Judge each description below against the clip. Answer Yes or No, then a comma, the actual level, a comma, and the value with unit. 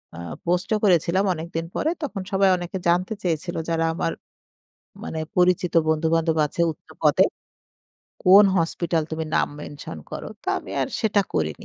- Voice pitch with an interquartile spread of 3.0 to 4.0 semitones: No, narrow, 2.4 semitones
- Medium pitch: Yes, medium, 170 Hz